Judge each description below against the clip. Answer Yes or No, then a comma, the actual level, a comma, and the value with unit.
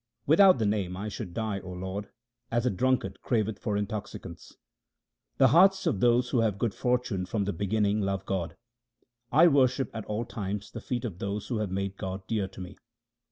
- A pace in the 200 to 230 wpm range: Yes, fast, 205 wpm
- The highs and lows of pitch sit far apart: No, average, 3.8 semitones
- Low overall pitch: Yes, low, 105 Hz